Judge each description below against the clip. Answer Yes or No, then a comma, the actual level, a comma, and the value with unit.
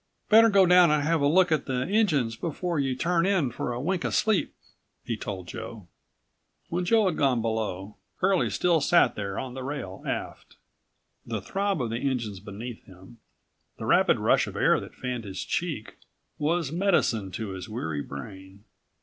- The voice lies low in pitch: Yes, low, 130 Hz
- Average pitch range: No, wide, 8.5 semitones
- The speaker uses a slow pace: No, average, 180 wpm